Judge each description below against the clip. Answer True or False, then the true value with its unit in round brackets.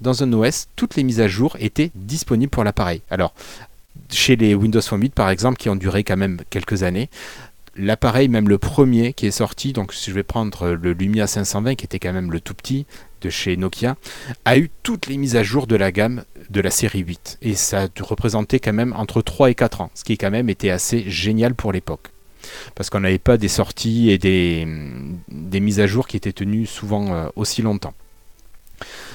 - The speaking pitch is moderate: False (105 Hz)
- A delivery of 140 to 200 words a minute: False (215 wpm)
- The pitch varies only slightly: False (3.7 semitones)